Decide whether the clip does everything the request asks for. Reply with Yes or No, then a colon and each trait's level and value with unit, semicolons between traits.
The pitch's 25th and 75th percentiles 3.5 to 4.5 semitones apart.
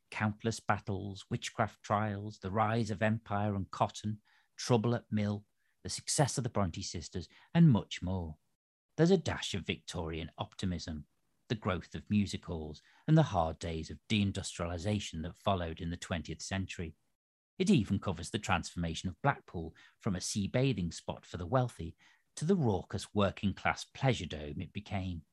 Yes: average, 3.9 semitones